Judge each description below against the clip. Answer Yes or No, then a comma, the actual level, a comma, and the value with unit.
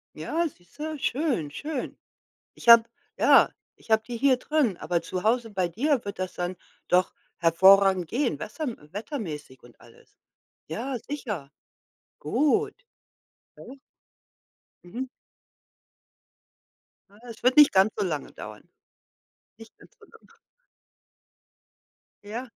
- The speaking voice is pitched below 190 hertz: No, high, 225 Hz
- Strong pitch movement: Yes, wide, 7.0 semitones